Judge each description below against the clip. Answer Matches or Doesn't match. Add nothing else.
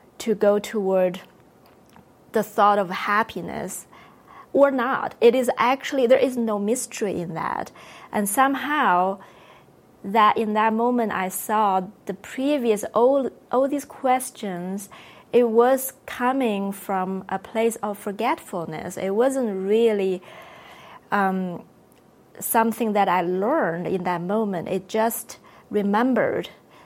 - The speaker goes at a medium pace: Doesn't match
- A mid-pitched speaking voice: Doesn't match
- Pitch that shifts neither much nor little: Matches